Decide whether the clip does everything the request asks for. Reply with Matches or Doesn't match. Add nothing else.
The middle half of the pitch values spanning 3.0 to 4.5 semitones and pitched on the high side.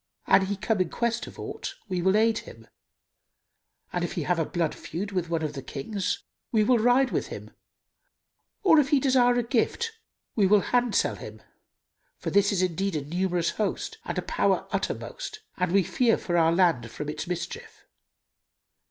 Doesn't match